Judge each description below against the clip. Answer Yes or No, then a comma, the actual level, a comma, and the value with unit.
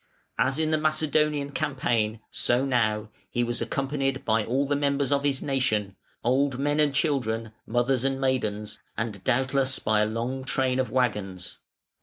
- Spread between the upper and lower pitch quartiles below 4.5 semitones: Yes, average, 3.7 semitones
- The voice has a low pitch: Yes, low, 130 Hz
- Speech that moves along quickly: No, average, 160 wpm